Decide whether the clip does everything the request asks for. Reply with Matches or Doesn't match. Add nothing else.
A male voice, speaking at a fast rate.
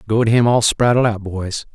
Matches